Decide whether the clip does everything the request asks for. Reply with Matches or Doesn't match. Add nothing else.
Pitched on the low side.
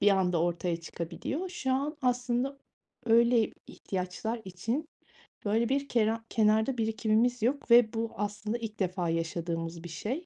Doesn't match